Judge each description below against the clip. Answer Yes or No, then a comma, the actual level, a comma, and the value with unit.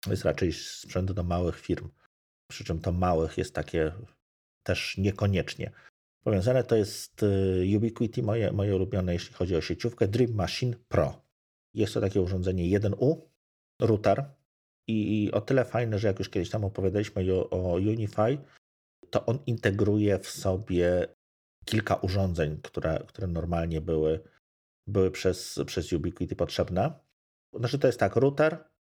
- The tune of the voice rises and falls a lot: No, average, 3.7 semitones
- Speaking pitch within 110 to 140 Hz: No, very low, 95 Hz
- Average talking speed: Yes, average, 140 wpm